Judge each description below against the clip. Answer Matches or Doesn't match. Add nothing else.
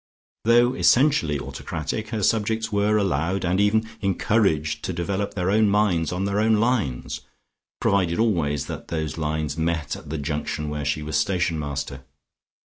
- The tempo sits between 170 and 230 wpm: Doesn't match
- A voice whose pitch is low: Matches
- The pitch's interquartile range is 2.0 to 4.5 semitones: Doesn't match